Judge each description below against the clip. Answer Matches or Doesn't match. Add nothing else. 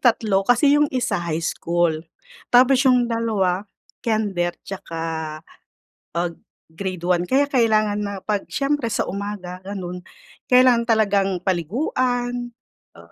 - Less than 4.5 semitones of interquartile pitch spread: Doesn't match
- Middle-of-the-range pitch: Doesn't match